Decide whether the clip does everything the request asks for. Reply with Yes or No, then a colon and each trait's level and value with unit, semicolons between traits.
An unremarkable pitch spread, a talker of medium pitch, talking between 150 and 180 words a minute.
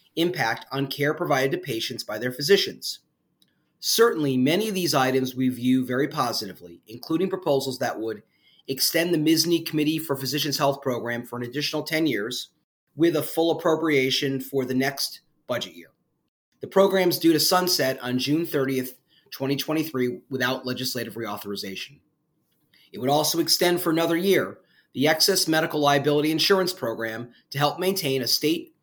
Yes: average, 4.2 semitones; medium, 145 Hz; average, 155 wpm